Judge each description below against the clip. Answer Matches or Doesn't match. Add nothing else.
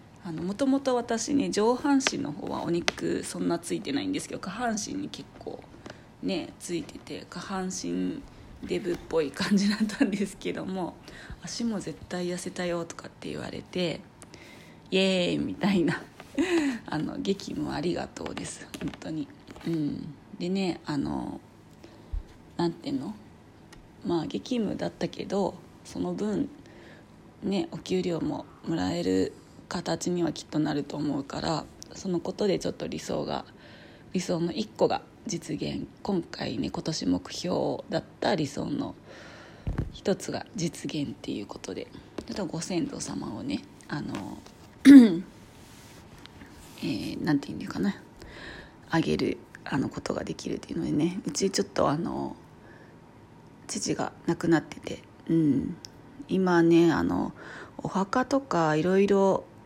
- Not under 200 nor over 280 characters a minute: Matches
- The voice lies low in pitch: Doesn't match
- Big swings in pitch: Matches